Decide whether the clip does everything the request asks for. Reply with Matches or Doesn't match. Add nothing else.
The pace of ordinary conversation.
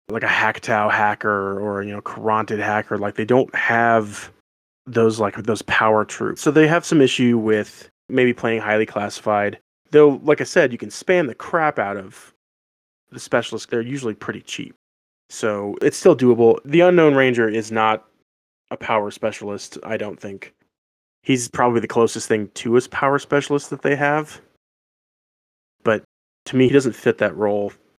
Matches